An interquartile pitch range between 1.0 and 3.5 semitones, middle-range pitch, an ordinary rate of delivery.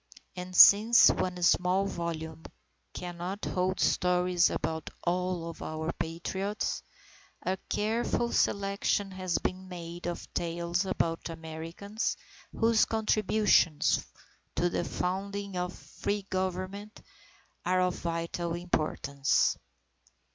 No: average, 2.7 semitones; medium, 180 Hz; slow, 105 wpm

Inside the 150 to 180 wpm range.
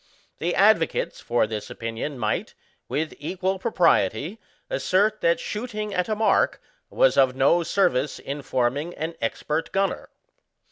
No: slow, 135 wpm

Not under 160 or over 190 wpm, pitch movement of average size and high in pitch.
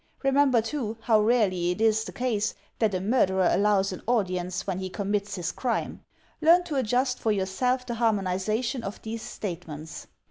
Yes: average, 170 wpm; average, 4.4 semitones; high, 215 Hz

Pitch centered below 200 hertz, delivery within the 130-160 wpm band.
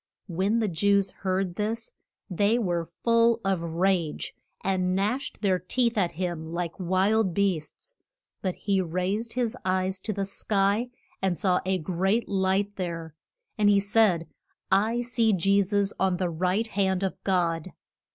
Yes: high, 190 Hz; average, 150 wpm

